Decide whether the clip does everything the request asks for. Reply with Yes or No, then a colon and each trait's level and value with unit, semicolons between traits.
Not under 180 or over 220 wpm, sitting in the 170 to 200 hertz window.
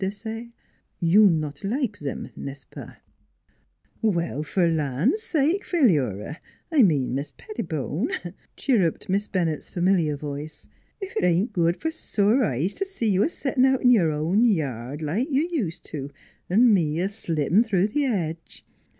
No: average, 170 wpm; medium, 185 Hz